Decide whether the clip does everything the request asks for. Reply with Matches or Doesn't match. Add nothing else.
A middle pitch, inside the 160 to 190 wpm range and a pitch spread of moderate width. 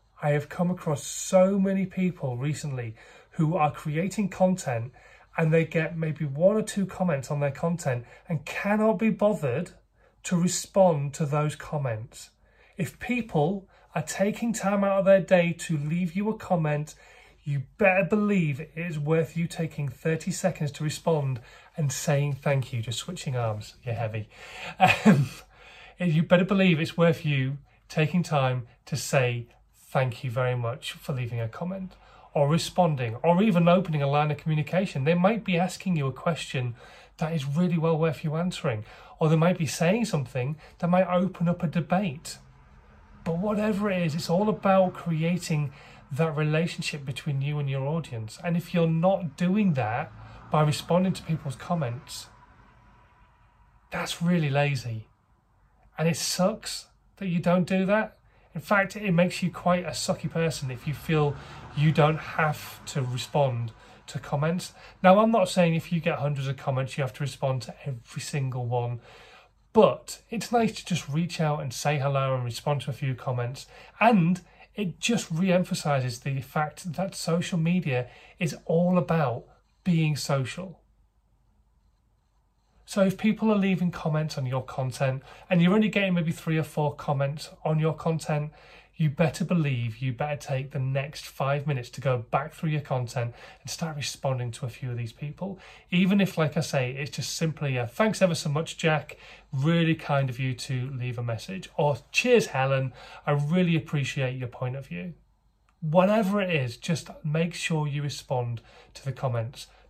Matches